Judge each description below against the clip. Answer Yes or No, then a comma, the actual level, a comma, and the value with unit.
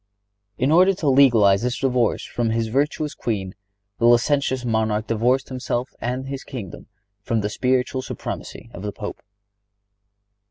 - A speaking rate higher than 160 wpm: No, average, 145 wpm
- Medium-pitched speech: No, low, 125 Hz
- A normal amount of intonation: Yes, average, 3.1 semitones